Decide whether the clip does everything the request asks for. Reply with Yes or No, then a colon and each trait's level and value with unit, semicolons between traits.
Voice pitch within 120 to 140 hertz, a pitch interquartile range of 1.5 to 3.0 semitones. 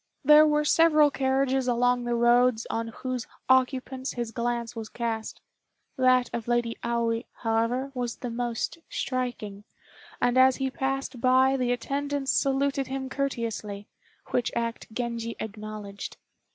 No: high, 245 Hz; narrow, 2.4 semitones